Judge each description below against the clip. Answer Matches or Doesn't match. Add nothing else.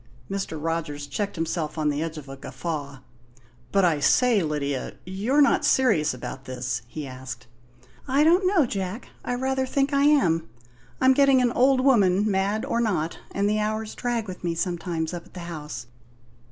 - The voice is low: Doesn't match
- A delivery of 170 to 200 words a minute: Matches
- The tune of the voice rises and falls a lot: Matches